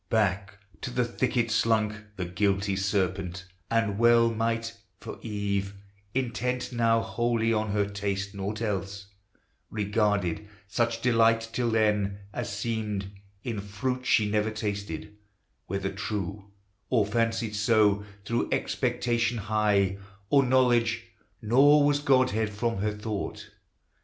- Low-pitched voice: Yes, low, 110 Hz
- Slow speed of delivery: Yes, slow, 120 wpm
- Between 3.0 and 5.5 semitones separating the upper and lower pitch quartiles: No, narrow, 2.5 semitones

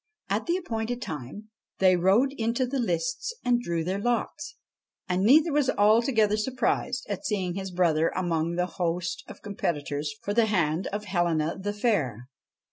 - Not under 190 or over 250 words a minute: No, average, 160 wpm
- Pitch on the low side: No, high, 200 Hz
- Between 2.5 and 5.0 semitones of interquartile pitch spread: No, wide, 5.6 semitones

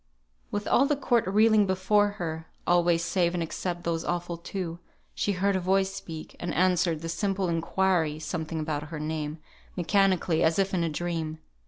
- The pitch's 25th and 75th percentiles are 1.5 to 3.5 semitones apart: Yes, average, 2.9 semitones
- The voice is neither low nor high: Yes, medium, 175 Hz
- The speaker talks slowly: No, average, 175 wpm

